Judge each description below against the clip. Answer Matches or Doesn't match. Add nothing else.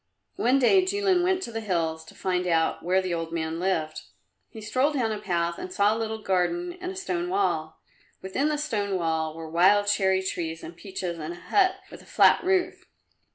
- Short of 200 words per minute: Doesn't match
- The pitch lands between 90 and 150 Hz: Doesn't match